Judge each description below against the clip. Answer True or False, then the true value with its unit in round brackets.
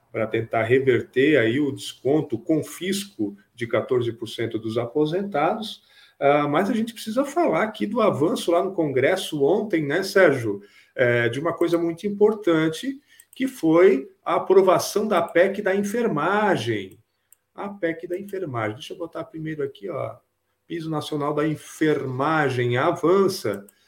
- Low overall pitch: False (165 Hz)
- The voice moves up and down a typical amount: False (6.1 semitones)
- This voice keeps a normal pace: True (140 wpm)